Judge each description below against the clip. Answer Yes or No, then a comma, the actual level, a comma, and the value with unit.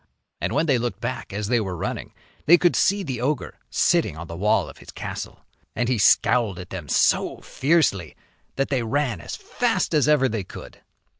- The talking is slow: No, average, 200 wpm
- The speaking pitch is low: Yes, low, 120 Hz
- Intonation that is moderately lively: No, wide, 6.7 semitones